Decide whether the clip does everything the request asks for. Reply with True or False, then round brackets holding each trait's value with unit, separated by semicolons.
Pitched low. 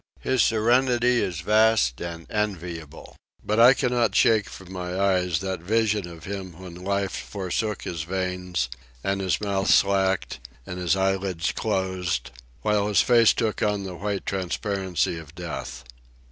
True (95 Hz)